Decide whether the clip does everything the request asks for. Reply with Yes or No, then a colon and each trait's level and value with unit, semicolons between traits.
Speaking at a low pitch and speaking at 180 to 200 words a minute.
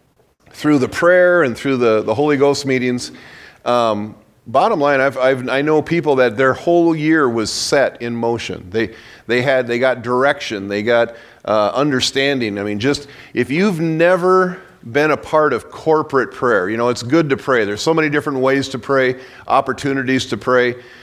Yes: low, 130 Hz; average, 185 wpm